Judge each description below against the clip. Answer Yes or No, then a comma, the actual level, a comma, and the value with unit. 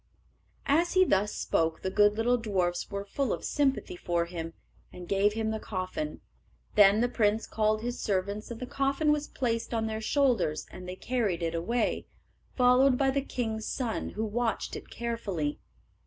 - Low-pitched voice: No, high, 220 Hz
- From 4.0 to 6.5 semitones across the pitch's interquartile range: Yes, average, 4.5 semitones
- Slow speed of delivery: No, average, 175 wpm